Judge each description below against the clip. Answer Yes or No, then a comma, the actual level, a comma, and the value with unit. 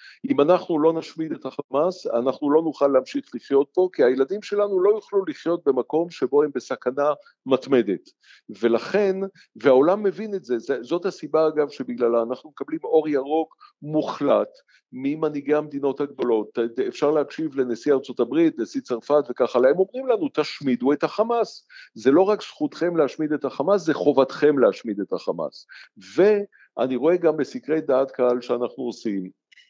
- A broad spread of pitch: Yes, wide, 6.4 semitones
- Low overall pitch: No, medium, 155 Hz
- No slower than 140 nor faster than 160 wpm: Yes, fast, 150 wpm